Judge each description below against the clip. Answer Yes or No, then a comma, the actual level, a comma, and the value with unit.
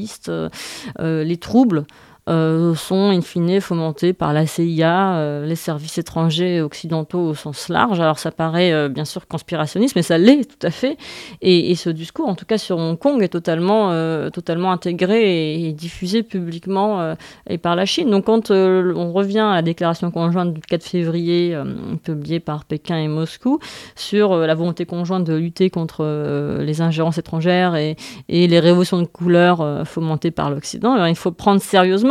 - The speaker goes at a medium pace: Yes, average, 190 wpm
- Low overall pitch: No, medium, 170 Hz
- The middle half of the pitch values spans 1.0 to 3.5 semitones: Yes, narrow, 2.4 semitones